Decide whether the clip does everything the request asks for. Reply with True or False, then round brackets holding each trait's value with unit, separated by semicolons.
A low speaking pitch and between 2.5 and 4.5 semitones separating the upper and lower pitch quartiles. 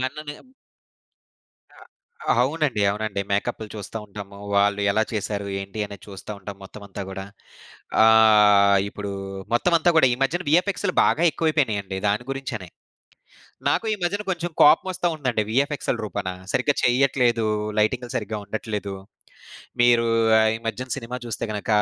False (110 Hz; 5.2 semitones)